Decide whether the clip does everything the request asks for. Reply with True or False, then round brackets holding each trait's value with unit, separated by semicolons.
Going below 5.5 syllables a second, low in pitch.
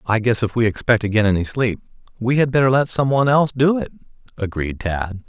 False (6.1 syllables/s; 120 Hz)